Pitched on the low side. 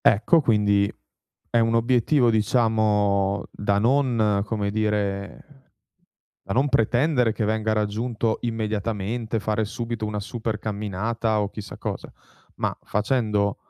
Yes: low, 110 Hz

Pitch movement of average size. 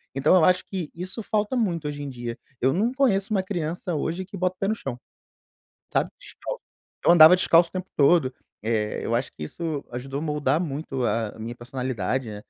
No: wide, 6.2 semitones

